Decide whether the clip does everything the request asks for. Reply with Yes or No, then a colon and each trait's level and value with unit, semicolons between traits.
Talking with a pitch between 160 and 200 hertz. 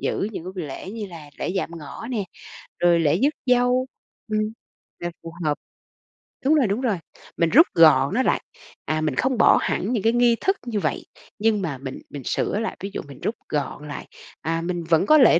Yes: high, 190 Hz